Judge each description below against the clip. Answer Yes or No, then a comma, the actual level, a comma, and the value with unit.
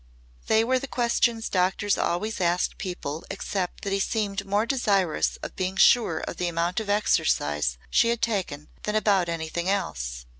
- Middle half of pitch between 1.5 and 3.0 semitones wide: No, average, 4.0 semitones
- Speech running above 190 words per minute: No, average, 165 wpm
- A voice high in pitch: Yes, high, 195 Hz